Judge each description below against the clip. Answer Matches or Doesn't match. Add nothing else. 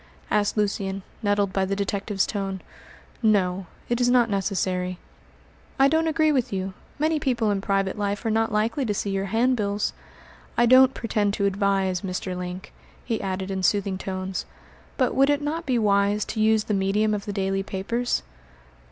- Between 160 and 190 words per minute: Matches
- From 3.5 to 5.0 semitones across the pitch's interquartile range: Doesn't match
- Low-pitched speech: Doesn't match